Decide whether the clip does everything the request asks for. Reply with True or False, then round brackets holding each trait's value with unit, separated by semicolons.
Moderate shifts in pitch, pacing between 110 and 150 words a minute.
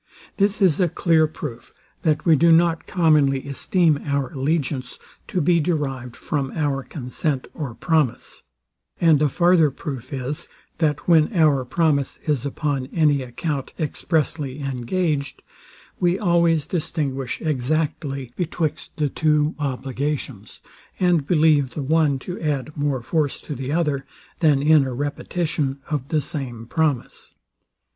True (3.1 semitones; 135 wpm)